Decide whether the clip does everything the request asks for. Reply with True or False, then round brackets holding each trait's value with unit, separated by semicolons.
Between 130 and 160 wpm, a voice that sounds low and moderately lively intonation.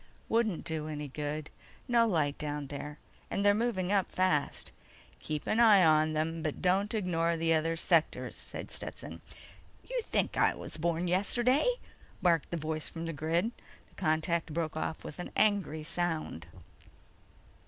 False (155 wpm; 165 Hz; 3.6 semitones)